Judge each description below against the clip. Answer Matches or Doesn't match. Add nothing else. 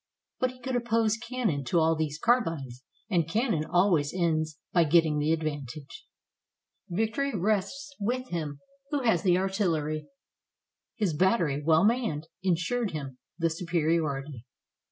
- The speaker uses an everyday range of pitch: Doesn't match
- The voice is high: Doesn't match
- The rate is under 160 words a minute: Matches